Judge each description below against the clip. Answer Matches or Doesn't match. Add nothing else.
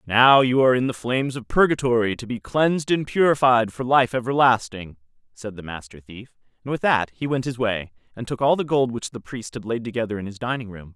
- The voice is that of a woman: Doesn't match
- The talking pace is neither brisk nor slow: Doesn't match